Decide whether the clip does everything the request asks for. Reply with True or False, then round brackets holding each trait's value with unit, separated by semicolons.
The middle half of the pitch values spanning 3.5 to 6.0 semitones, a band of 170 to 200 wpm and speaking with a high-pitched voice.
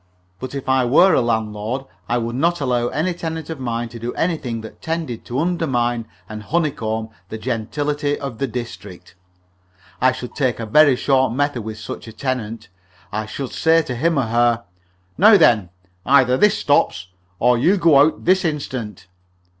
False (4.5 semitones; 175 wpm; 125 Hz)